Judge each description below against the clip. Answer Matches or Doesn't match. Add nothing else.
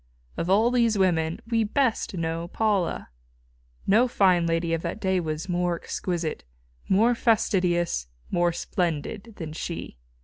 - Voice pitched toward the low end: Doesn't match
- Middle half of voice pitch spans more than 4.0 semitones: Matches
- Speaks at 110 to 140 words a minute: Matches